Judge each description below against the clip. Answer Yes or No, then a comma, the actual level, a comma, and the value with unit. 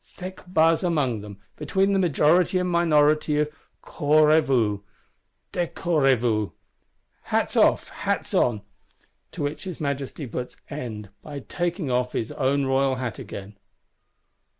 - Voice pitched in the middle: Yes, medium, 145 Hz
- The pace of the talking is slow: Yes, slow, 125 wpm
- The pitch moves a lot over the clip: No, average, 4.8 semitones